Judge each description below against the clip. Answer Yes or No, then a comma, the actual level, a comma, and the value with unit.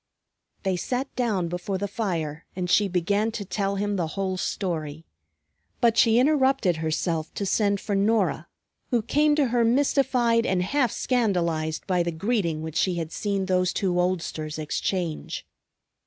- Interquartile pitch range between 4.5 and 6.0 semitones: Yes, average, 5.0 semitones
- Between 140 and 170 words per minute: Yes, average, 155 wpm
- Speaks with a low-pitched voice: No, high, 195 Hz